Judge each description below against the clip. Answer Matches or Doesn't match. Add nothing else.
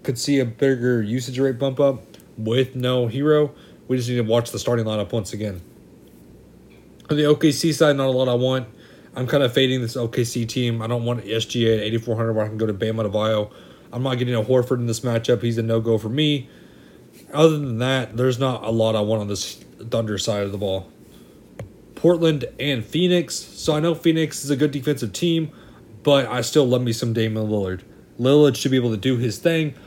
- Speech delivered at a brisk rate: Matches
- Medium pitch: Doesn't match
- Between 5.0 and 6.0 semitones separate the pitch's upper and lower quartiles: Doesn't match